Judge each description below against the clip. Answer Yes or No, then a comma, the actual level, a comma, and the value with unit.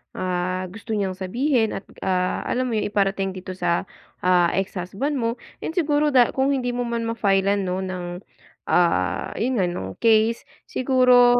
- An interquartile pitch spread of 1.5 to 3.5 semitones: No, average, 4.9 semitones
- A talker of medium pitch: No, high, 205 Hz